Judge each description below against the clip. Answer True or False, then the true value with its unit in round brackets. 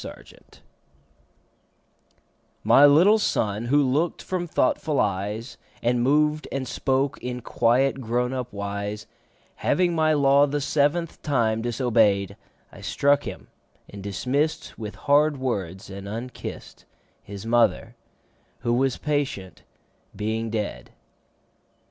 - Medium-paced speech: False (120 wpm)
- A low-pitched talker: True (125 Hz)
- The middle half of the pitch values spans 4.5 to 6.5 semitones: True (4.8 semitones)